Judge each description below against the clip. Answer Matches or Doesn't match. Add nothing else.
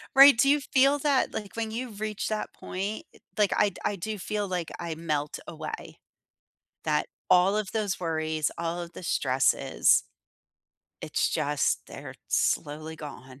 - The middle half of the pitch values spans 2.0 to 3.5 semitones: Doesn't match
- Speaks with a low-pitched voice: Doesn't match